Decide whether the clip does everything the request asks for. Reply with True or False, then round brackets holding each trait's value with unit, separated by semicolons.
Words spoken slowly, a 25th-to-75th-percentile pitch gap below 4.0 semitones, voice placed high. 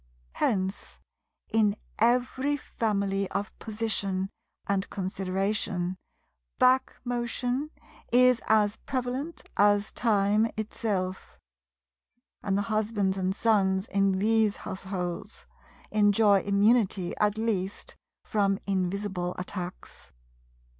True (90 wpm; 2.7 semitones; 205 Hz)